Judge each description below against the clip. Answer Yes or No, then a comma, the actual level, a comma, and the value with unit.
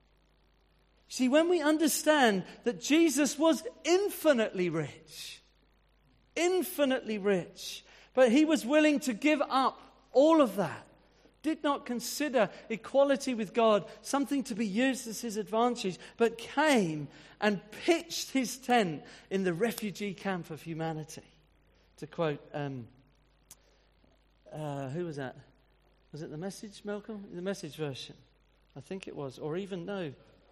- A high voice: Yes, high, 210 Hz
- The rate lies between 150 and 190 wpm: No, slow, 135 wpm